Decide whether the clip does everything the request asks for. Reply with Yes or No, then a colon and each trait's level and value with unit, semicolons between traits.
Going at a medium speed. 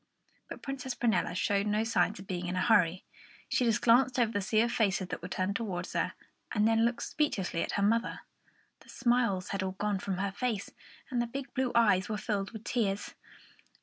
No: fast, 210 wpm